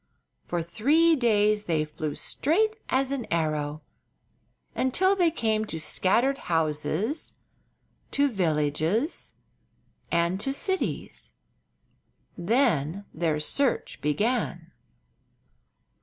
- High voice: Yes, high, 205 Hz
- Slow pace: Yes, slow, 90 wpm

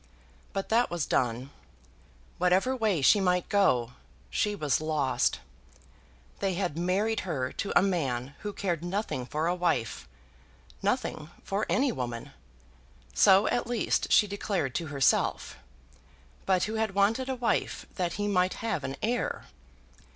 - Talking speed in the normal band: Yes, average, 145 wpm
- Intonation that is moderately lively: No, wide, 5.8 semitones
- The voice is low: No, medium, 180 Hz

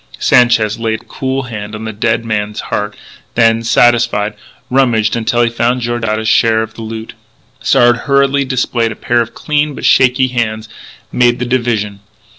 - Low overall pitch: Yes, low, 115 Hz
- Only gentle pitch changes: Yes, narrow, 1.9 semitones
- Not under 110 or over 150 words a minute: No, average, 165 wpm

